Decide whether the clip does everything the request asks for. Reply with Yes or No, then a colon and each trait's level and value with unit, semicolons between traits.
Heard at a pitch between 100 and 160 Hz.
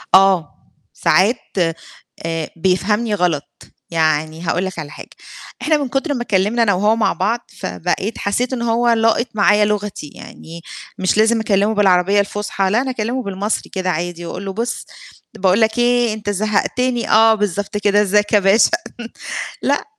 No: high, 205 Hz